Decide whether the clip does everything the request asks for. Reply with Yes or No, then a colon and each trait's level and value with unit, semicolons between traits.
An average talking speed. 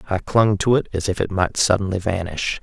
No: fast, 230 wpm